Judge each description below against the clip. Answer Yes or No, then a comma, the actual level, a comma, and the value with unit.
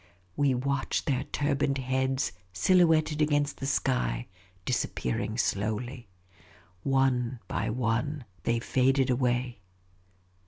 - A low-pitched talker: Yes, low, 130 Hz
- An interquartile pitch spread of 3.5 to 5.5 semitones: No, narrow, 2.4 semitones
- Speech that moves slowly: Yes, slow, 105 wpm